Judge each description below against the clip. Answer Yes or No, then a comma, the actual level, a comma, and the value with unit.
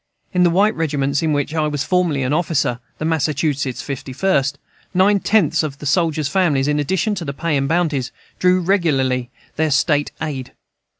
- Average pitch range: Yes, average, 3.8 semitones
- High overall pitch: No, medium, 155 Hz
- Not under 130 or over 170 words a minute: No, average, 180 wpm